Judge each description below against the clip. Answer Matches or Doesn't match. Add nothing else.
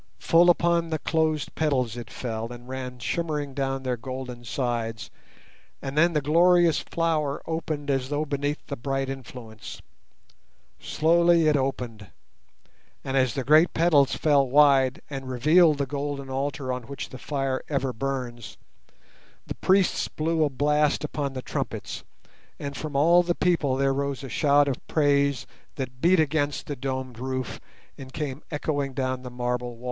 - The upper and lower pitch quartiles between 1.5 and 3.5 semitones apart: Matches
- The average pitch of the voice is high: Doesn't match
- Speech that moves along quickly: Doesn't match